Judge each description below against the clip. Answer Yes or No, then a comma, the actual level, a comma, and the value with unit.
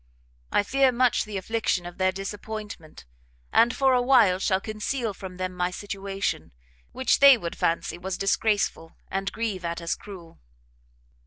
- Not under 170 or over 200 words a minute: No, average, 155 wpm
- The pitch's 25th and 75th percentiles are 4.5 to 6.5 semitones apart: No, average, 3.7 semitones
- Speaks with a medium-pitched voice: No, high, 195 Hz